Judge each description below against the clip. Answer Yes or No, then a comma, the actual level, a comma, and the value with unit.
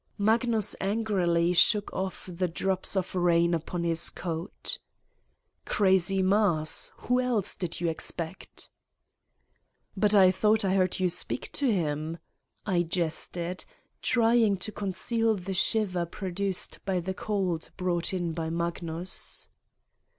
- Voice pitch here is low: No, medium, 185 Hz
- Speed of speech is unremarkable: No, slow, 125 wpm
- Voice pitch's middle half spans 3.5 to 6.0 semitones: No, average, 3.1 semitones